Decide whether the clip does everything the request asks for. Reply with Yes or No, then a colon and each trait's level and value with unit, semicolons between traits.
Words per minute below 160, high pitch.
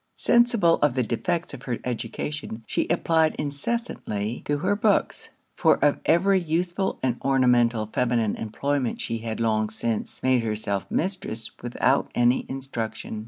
No: average, 140 wpm; low, 130 Hz